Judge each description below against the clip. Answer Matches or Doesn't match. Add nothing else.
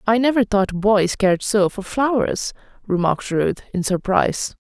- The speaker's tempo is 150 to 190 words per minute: Matches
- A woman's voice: Matches